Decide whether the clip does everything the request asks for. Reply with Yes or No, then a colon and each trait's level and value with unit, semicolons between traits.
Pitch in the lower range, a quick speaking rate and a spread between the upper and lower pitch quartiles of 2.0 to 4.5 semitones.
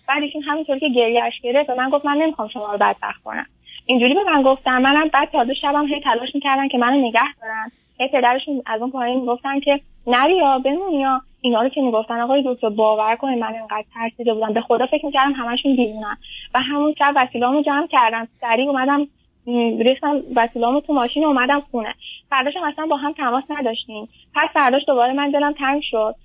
No: very high, 260 Hz; fast, 195 wpm; average, 3.3 semitones